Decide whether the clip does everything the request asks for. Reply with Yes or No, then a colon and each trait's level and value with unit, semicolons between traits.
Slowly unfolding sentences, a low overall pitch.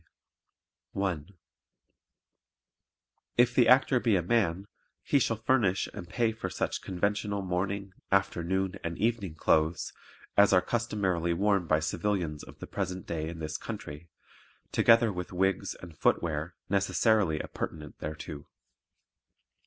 Yes: slow, 125 wpm; very low, 95 Hz